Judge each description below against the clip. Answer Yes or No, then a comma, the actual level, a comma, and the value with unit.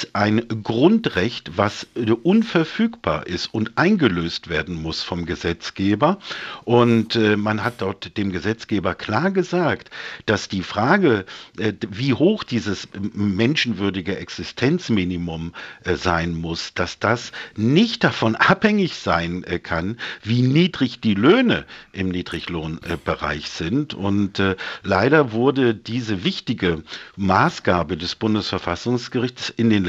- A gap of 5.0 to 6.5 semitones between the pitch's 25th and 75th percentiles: Yes, wide, 5.6 semitones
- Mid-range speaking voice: No, low, 105 Hz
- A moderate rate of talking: No, slow, 105 wpm